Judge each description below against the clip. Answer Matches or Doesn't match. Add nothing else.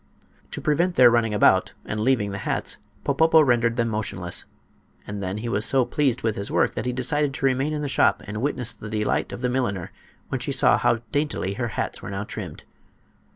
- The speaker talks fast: Matches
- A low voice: Matches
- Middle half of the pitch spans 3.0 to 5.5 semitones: Matches